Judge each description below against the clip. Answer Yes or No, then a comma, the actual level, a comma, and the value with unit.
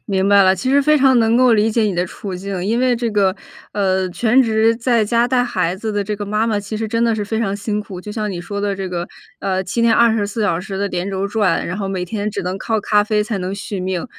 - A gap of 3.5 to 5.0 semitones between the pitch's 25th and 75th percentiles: No, average, 2.8 semitones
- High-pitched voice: Yes, high, 205 Hz